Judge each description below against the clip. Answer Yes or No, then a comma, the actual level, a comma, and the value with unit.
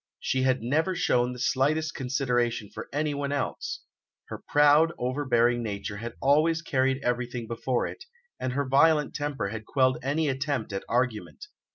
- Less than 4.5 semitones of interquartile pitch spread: Yes, average, 3.3 semitones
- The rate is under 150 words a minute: No, average, 155 wpm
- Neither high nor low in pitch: No, low, 130 Hz